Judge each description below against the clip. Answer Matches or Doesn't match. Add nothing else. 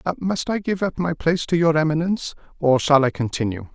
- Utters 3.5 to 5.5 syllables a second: Doesn't match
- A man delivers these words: Matches